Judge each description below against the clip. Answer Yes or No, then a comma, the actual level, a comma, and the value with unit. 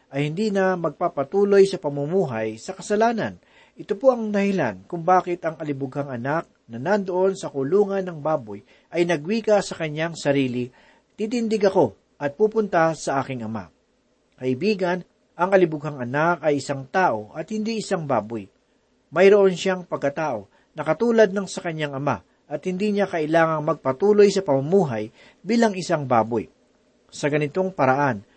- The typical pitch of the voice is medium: Yes, medium, 165 Hz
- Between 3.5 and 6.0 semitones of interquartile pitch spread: Yes, wide, 5.6 semitones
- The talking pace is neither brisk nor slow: Yes, average, 145 wpm